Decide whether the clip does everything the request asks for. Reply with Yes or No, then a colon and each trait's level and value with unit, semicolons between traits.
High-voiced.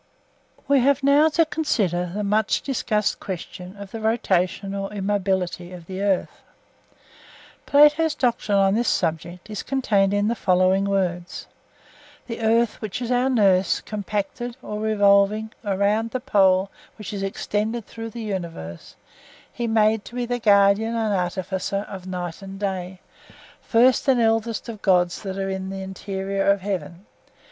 Yes: high, 200 Hz